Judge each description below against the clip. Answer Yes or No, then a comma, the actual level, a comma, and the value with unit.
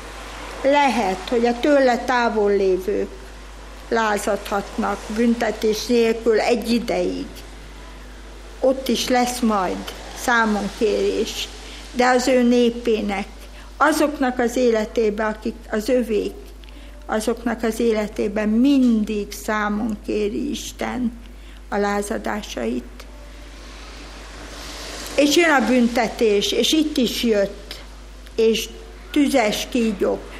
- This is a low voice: No, high, 235 Hz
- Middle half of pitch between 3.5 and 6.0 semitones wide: No, average, 2.7 semitones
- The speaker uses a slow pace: Yes, slow, 90 wpm